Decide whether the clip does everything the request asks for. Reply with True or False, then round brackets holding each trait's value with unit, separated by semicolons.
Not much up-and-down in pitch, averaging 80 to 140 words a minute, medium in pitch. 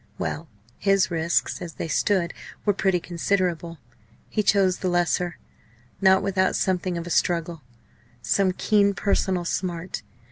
True (2.3 semitones; 135 wpm; 180 Hz)